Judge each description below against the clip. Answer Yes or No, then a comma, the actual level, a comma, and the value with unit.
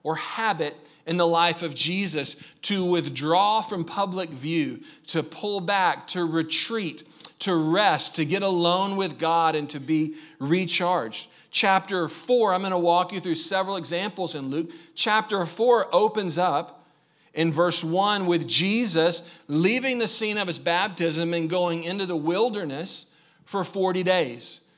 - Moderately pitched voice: Yes, medium, 175 Hz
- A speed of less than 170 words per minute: Yes, average, 150 wpm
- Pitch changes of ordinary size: Yes, average, 3.0 semitones